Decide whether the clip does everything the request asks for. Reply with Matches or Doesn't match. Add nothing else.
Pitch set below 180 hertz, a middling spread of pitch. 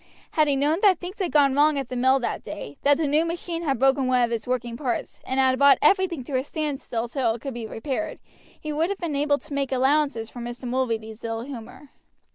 Doesn't match